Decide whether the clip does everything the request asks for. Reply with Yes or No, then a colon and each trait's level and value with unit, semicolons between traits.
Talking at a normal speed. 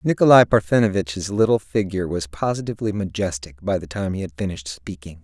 Yes: average, 160 wpm